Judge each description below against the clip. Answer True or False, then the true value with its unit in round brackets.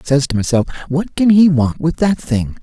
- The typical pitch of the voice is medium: True (150 Hz)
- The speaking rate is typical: False (250 wpm)